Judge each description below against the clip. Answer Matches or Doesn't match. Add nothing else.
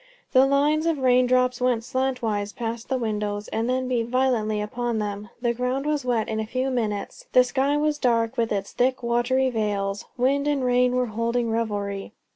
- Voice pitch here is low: Doesn't match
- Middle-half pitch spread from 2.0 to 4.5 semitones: Matches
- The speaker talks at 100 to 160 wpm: Doesn't match